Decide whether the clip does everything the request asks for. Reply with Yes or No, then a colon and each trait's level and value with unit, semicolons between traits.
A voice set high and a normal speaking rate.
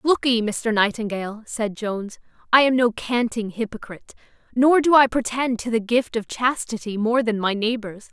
Yes: high, 230 Hz; average, 170 wpm